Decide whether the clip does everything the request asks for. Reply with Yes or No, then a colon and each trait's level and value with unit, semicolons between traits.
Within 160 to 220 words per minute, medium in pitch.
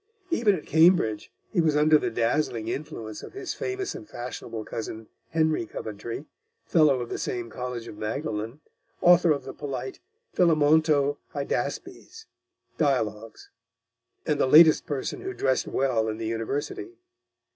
No: average, 140 wpm; medium, 145 Hz